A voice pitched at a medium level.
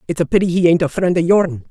Yes: medium, 175 Hz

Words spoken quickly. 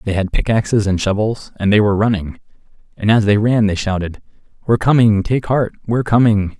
No: average, 190 wpm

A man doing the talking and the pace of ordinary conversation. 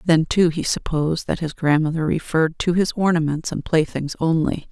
No: female; average, 180 wpm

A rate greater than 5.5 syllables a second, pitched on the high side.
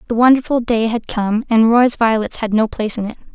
Yes: 5.7 syllables/s; high, 225 Hz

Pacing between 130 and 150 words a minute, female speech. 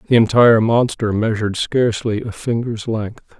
No: average, 140 wpm; male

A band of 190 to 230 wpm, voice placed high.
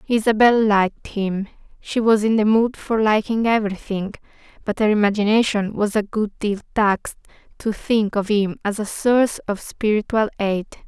No: average, 155 wpm; high, 210 Hz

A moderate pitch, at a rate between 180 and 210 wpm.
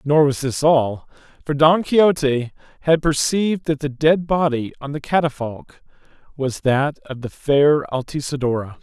No: medium, 145 Hz; average, 150 wpm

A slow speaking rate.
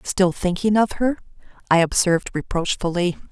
Yes: slow, 125 wpm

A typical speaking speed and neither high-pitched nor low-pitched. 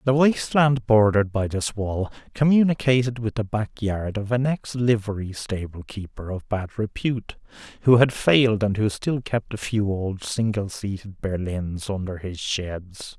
No: average, 170 wpm; low, 110 Hz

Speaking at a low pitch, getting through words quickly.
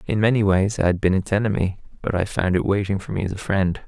Yes: low, 100 Hz; fast, 280 wpm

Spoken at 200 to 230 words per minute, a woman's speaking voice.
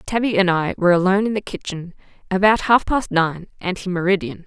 No: average, 190 wpm; female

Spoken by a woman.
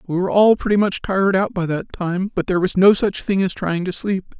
No: male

